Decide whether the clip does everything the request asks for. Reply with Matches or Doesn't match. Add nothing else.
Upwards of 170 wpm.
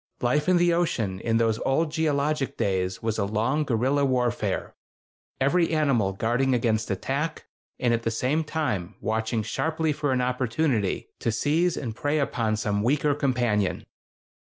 Doesn't match